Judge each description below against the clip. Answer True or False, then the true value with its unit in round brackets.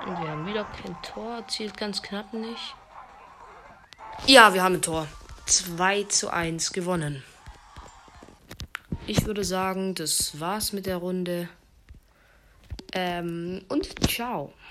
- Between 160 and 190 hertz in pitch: True (185 Hz)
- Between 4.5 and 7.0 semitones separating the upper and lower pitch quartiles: False (3.4 semitones)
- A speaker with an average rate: False (120 wpm)